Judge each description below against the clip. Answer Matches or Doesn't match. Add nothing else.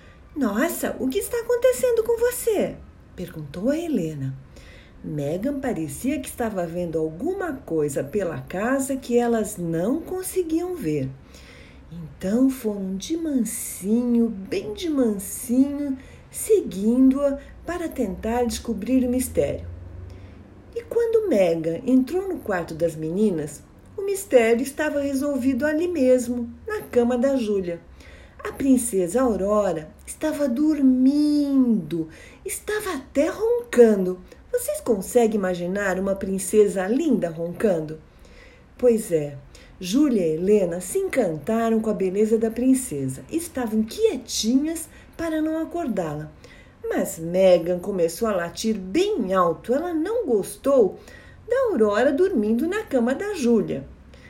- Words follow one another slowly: Matches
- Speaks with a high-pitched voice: Matches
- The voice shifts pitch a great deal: Matches